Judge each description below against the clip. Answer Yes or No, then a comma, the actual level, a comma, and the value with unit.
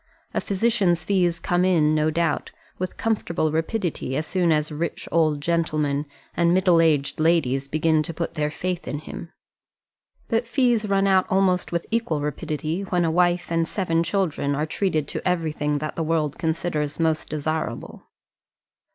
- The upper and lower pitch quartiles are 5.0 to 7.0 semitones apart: No, average, 2.9 semitones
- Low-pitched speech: No, medium, 165 Hz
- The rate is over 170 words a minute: No, average, 160 wpm